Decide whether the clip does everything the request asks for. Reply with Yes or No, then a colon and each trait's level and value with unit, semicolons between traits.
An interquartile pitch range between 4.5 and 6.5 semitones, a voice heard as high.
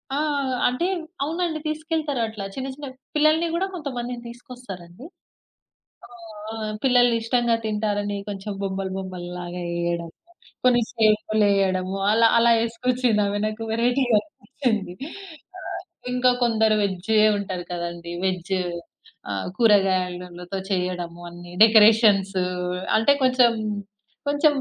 Yes: average, 4.9 semitones; high, 215 Hz